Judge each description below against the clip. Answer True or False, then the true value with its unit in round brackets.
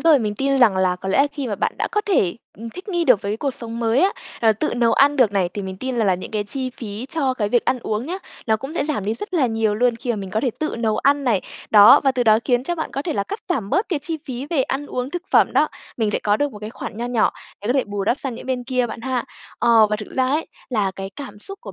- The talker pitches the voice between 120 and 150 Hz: False (245 Hz)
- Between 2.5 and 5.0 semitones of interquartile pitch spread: True (4.6 semitones)